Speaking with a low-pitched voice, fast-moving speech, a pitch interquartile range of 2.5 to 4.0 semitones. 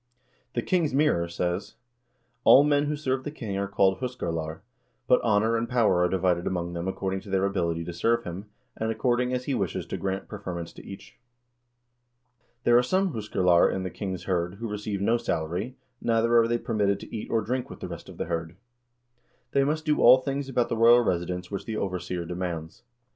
No: low, 105 Hz; fast, 210 wpm; average, 5.3 semitones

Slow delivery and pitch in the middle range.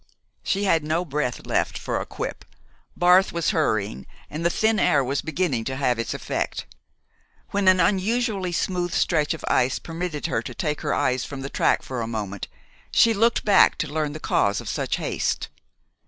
No: average, 185 wpm; medium, 160 Hz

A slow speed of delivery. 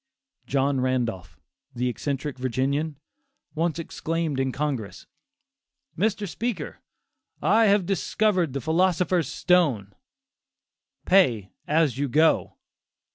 Yes: slow, 95 wpm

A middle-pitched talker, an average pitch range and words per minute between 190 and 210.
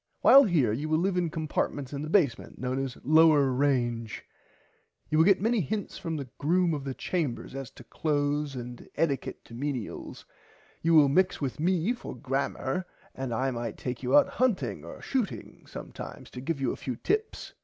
Yes: medium, 145 Hz; average, 4.6 semitones; average, 195 wpm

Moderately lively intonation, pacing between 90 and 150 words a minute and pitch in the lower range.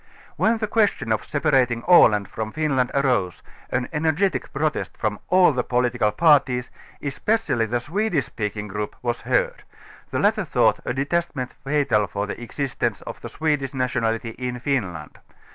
Yes: average, 4.9 semitones; average, 140 wpm; low, 130 Hz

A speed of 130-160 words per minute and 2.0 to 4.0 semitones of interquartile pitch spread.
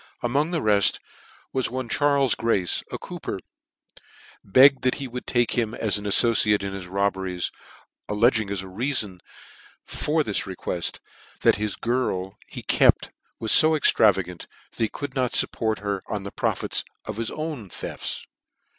No: average, 155 wpm; average, 4.7 semitones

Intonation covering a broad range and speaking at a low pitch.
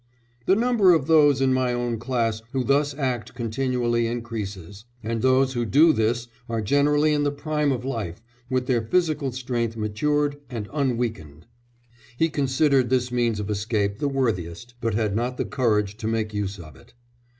No: average, 4.0 semitones; low, 120 Hz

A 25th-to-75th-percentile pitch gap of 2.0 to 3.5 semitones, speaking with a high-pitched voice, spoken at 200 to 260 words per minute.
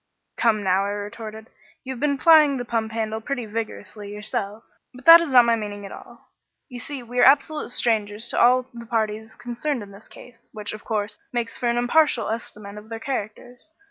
Yes: average, 2.8 semitones; high, 230 Hz; fast, 205 wpm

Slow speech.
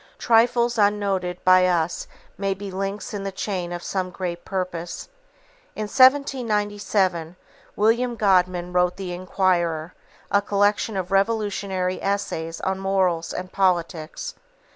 Yes: slow, 120 wpm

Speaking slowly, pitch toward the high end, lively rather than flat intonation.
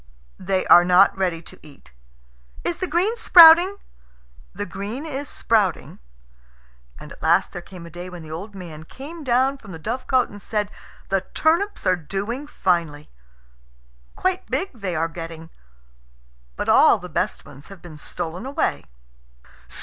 No: average, 155 wpm; high, 195 Hz; wide, 8.1 semitones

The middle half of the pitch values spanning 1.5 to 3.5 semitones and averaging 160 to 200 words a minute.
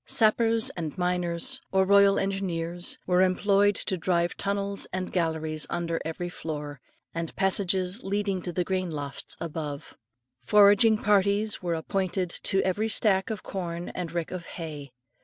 No: average, 2.9 semitones; average, 145 wpm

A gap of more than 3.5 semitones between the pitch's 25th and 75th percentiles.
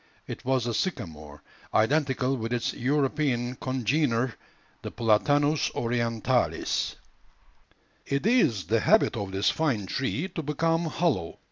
Yes: average, 4.7 semitones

